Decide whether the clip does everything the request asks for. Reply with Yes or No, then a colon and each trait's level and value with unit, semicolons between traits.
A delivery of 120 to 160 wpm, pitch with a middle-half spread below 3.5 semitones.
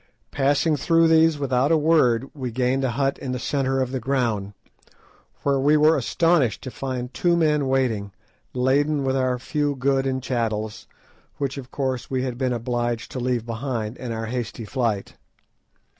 No: average, 175 wpm; average, 2.7 semitones